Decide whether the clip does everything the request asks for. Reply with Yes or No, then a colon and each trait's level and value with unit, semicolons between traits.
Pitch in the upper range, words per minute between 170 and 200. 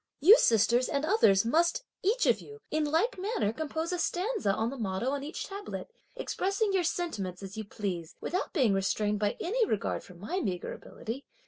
Yes: very high, 285 Hz; average, 190 wpm